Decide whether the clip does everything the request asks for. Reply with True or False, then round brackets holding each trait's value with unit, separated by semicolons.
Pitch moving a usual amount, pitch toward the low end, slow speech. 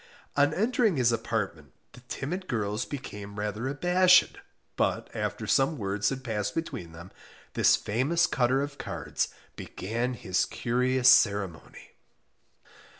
False (5.7 semitones; 120 Hz; 125 wpm)